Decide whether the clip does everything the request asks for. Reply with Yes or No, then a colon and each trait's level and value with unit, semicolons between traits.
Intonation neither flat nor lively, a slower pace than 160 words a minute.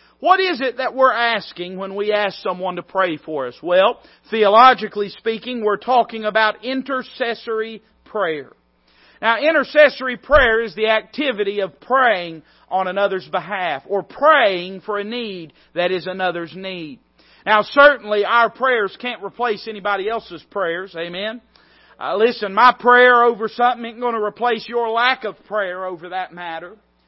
Yes: average, 4.5 semitones; average, 150 wpm